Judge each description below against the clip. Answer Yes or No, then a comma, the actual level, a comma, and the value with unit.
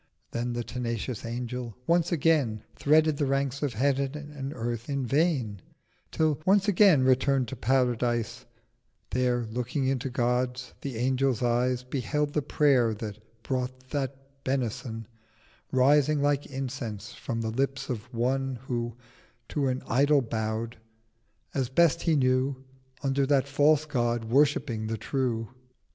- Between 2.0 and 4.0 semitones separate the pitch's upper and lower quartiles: Yes, average, 2.9 semitones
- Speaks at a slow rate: Yes, slow, 130 wpm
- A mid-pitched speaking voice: No, low, 130 Hz